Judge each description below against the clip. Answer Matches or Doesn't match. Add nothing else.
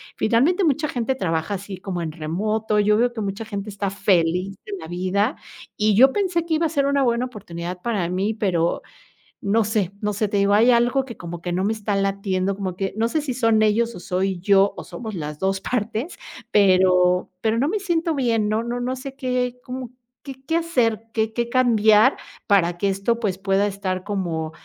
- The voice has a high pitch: Matches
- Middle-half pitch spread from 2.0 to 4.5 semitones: Matches